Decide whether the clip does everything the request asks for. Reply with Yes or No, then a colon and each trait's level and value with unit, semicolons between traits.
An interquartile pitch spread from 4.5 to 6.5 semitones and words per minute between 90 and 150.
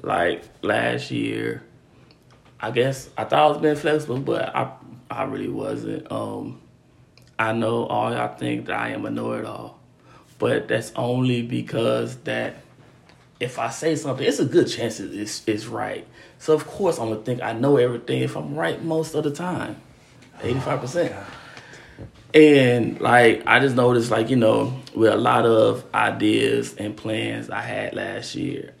No: average, 4.8 semitones; average, 165 wpm